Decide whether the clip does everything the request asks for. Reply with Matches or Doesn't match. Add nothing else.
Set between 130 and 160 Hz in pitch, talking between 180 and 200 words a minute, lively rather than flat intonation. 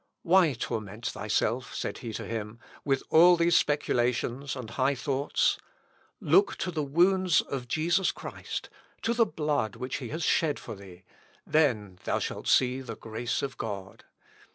Doesn't match